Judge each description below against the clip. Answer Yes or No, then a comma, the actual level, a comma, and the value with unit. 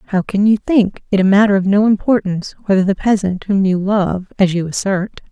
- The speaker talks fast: Yes, fast, 215 wpm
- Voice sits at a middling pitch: No, high, 195 Hz